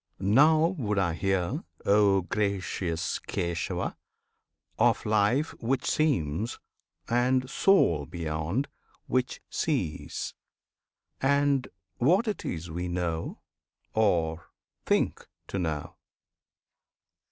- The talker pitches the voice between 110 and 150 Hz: No, low, 100 Hz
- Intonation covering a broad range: Yes, wide, 7.3 semitones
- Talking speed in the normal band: No, slow, 90 wpm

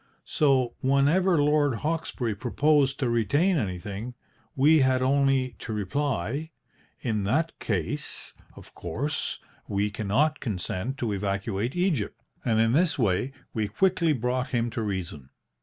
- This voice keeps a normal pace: No, slow, 130 wpm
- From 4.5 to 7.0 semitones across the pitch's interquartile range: Yes, wide, 5.6 semitones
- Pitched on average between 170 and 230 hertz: No, low, 130 Hz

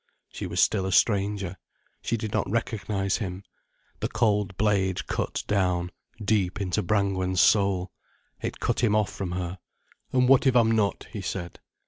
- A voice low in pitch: Yes, low, 100 Hz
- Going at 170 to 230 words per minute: No, average, 160 wpm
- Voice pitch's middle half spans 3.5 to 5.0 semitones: No, narrow, 2.5 semitones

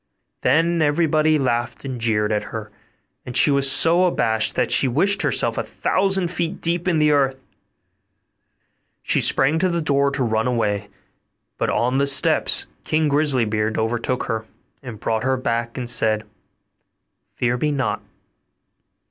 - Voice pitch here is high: No, low, 130 Hz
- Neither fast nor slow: Yes, average, 155 wpm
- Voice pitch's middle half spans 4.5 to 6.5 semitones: Yes, average, 5.0 semitones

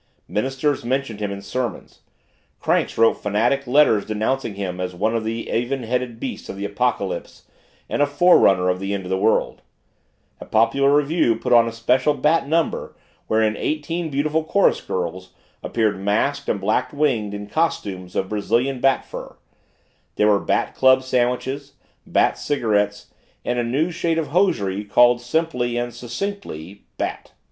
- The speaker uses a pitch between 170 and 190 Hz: No, low, 120 Hz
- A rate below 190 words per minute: Yes, average, 160 wpm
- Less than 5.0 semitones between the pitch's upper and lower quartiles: No, average, 5.3 semitones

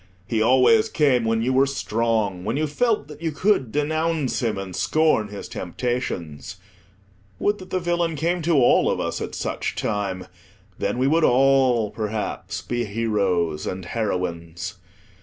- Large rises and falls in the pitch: Yes, wide, 7.2 semitones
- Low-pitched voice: Yes, low, 120 Hz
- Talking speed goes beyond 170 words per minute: No, average, 160 wpm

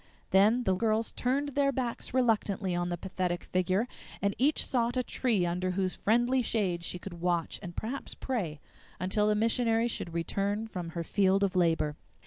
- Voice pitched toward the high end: Yes, high, 200 Hz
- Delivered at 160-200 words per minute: Yes, average, 175 wpm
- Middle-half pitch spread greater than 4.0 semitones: Yes, average, 4.7 semitones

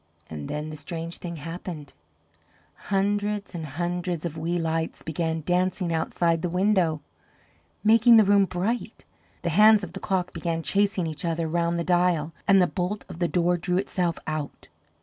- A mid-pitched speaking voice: Yes, medium, 175 Hz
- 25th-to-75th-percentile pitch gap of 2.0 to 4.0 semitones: Yes, average, 2.7 semitones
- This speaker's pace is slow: No, average, 170 wpm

